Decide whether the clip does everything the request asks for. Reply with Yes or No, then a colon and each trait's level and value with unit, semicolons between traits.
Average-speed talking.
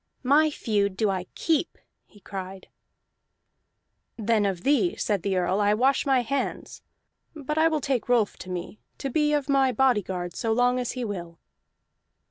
Yes: average, 165 wpm